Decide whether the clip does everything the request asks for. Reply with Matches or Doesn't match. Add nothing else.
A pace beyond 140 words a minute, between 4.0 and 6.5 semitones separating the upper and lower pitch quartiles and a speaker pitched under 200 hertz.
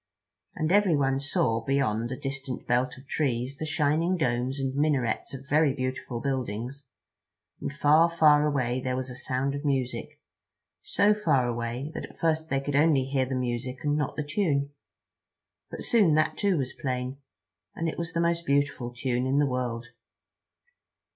Doesn't match